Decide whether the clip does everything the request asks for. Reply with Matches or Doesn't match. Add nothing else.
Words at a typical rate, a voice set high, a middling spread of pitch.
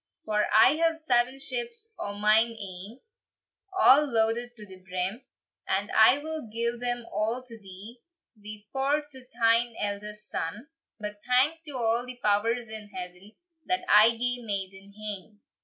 Matches